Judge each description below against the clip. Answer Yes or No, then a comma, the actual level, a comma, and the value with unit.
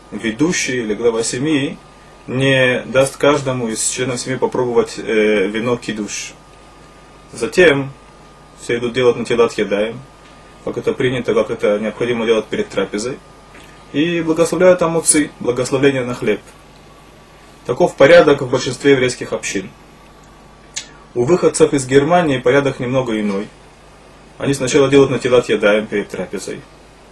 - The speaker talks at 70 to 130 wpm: Yes, average, 125 wpm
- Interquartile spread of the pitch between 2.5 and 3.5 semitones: Yes, average, 3.2 semitones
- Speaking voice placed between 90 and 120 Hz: No, low, 130 Hz